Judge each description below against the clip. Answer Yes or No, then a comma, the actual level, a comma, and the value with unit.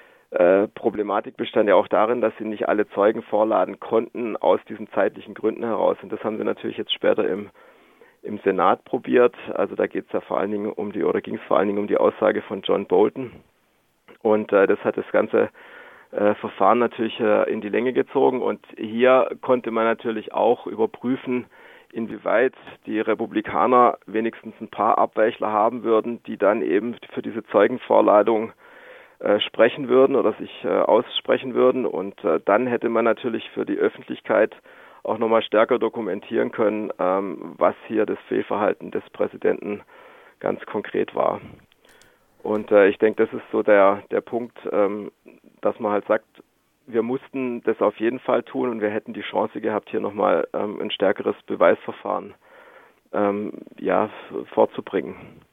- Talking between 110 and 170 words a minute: Yes, average, 165 wpm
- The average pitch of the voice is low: Yes, low, 120 Hz